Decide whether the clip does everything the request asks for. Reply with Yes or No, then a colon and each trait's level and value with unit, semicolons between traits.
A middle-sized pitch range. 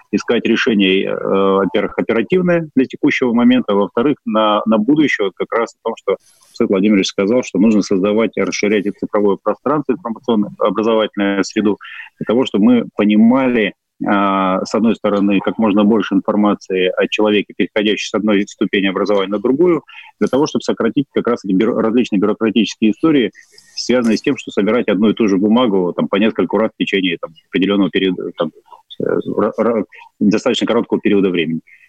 Yes: average, 4.7 semitones